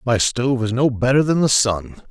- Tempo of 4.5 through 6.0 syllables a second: Yes, 5.1 syllables/s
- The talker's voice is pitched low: Yes, low, 120 Hz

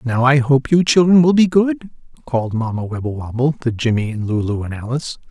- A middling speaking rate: Yes, average, 190 wpm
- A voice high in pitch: No, low, 135 Hz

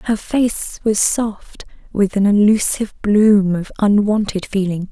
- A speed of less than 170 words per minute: Yes, slow, 135 wpm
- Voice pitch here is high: Yes, high, 205 Hz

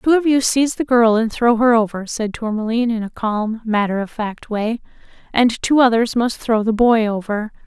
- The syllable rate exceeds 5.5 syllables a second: No, 5.1 syllables/s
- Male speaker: No, female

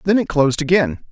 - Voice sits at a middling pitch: Yes, medium, 155 Hz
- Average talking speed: No, fast, 215 wpm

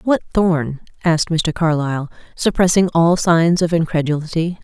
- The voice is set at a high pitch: No, medium, 165 Hz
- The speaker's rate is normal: No, slow, 130 wpm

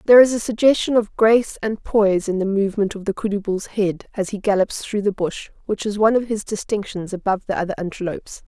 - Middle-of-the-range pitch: No, high, 205 Hz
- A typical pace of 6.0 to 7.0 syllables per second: Yes, 6.1 syllables/s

